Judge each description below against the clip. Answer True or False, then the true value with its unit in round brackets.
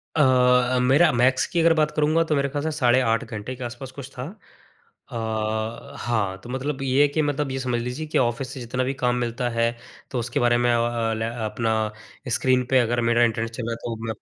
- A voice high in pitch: False (125 Hz)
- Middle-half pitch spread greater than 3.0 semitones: False (2.7 semitones)